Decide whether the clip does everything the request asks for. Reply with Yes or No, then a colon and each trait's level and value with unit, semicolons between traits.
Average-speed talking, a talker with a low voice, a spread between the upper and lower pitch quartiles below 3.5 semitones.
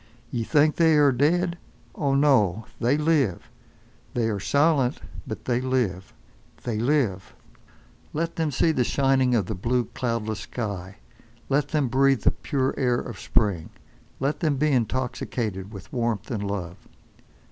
No: average, 145 wpm; low, 125 Hz; average, 5.1 semitones